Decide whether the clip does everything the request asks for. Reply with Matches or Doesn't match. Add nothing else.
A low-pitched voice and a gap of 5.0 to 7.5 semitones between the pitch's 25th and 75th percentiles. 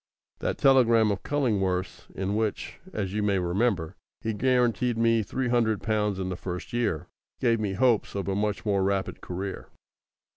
Doesn't match